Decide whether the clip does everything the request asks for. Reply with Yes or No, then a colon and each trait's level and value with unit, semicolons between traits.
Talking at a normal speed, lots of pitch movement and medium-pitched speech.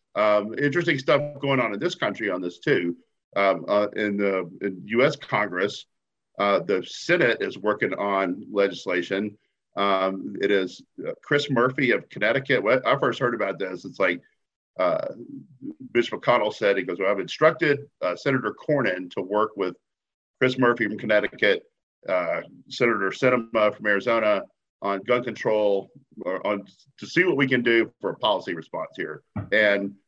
No: average, 165 wpm; wide, 5.8 semitones; low, 105 Hz